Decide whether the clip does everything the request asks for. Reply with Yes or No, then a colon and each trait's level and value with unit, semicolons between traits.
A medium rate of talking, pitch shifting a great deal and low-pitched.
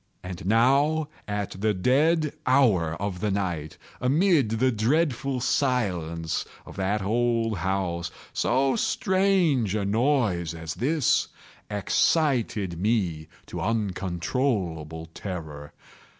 No: slow, 105 wpm; wide, 6.7 semitones; low, 105 Hz